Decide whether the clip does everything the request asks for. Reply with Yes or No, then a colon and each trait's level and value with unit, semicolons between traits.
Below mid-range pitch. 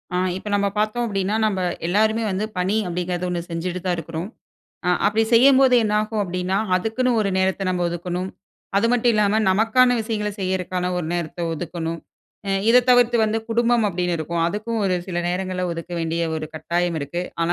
No: high, 190 Hz